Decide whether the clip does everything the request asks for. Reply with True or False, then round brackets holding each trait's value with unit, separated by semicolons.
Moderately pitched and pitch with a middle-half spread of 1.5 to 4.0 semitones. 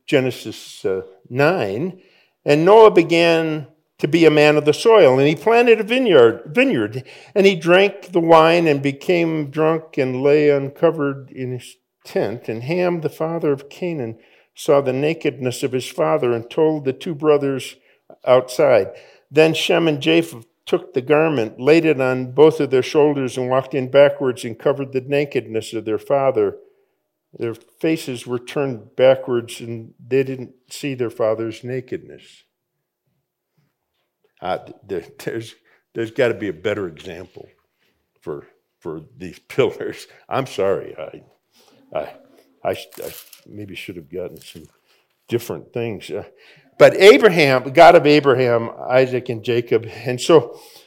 False (145 Hz; 4.8 semitones)